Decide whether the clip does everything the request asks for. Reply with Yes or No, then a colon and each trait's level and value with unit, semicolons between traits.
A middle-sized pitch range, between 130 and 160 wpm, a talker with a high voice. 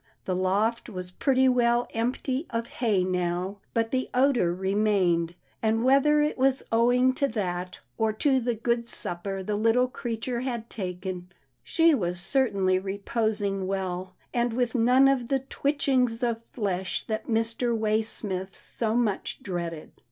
Yes: average, 4.7 semitones; average, 150 wpm; high, 225 Hz